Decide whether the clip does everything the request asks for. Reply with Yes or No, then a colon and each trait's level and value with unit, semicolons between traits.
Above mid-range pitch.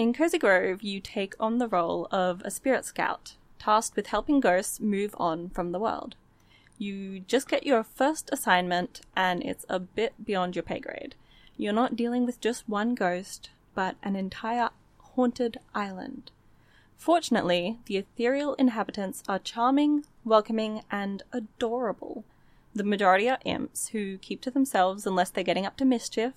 Yes: high, 215 Hz